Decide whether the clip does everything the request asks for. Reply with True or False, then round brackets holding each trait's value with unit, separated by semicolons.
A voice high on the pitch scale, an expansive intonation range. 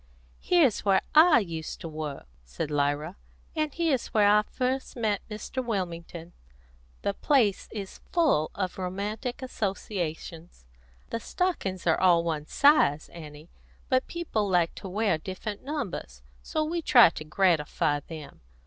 True (195 Hz; 7.5 semitones)